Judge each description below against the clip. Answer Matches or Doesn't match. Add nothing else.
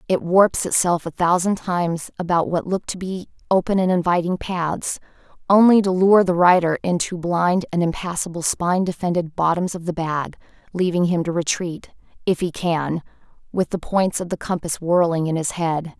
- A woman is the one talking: Matches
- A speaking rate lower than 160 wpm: Doesn't match